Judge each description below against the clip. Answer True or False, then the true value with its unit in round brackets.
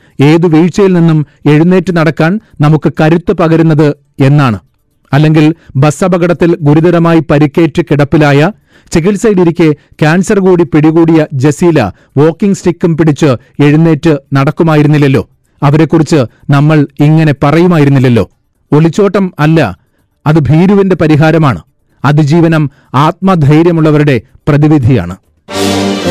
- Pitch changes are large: False (2.7 semitones)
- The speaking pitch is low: False (155 Hz)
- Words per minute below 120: True (85 wpm)